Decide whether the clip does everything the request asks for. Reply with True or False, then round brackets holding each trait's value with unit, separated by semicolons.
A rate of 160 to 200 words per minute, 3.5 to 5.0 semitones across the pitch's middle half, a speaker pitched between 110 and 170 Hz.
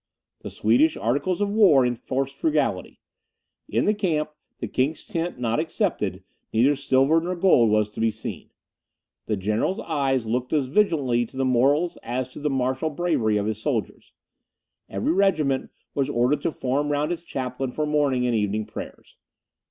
True (165 wpm; 4.6 semitones; 135 Hz)